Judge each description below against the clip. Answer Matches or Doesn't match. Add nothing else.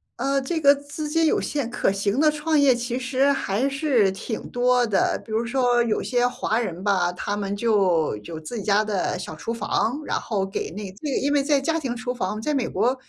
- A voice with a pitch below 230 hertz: Doesn't match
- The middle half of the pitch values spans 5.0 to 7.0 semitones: Matches